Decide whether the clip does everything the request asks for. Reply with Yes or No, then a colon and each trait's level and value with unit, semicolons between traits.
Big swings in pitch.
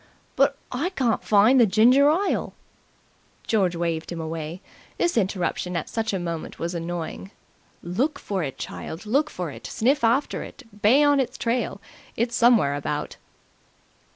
Yes: wide, 6.9 semitones